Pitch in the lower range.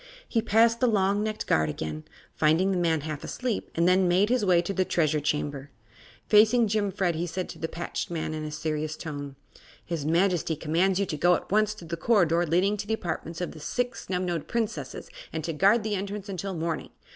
No: medium, 175 Hz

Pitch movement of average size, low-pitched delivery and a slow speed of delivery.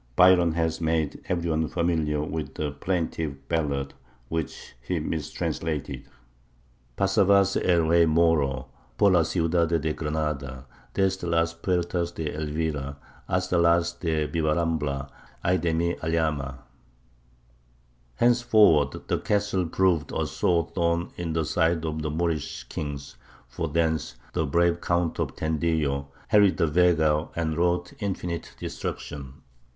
No: narrow, 2.2 semitones; very low, 80 Hz; slow, 125 wpm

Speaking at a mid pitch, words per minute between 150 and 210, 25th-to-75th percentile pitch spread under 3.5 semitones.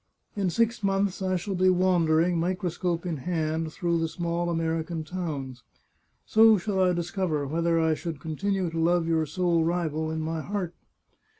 Yes: medium, 170 Hz; average, 165 wpm; narrow, 2.4 semitones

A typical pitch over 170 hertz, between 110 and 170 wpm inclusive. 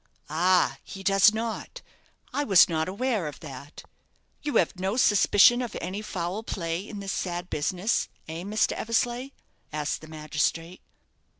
Yes: high, 190 Hz; average, 145 wpm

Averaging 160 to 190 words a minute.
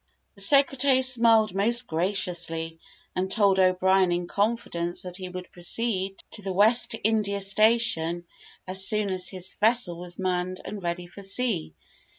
No: average, 150 wpm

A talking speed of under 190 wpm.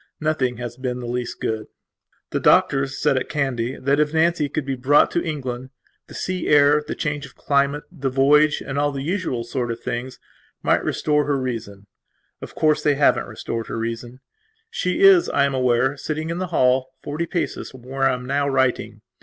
No: average, 195 wpm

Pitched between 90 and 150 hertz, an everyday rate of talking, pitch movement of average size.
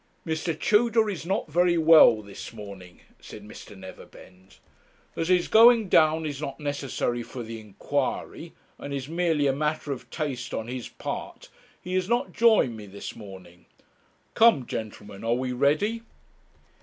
No: medium, 140 Hz; average, 155 wpm; wide, 7.6 semitones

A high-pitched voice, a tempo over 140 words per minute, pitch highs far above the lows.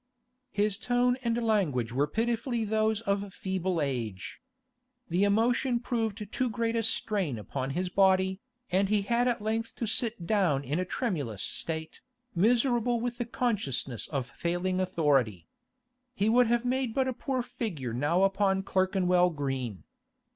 Yes: high, 200 Hz; average, 150 wpm; wide, 6.3 semitones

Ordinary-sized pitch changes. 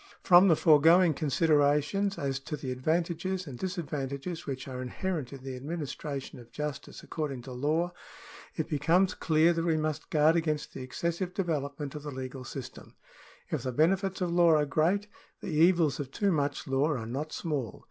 Yes: average, 3.8 semitones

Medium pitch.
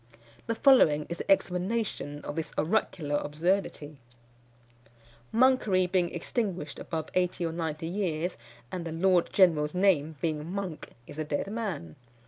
Yes: medium, 170 Hz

